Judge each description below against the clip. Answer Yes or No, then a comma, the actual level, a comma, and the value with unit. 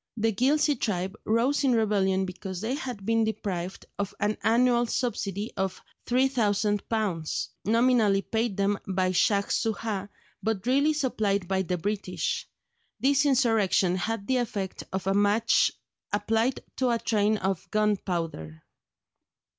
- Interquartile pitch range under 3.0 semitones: No, average, 3.4 semitones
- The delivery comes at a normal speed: No, slow, 130 wpm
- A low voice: No, high, 210 Hz